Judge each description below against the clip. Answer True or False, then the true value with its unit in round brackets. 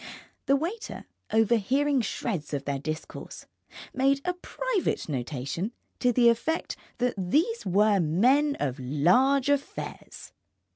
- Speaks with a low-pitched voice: False (235 Hz)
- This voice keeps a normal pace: False (115 wpm)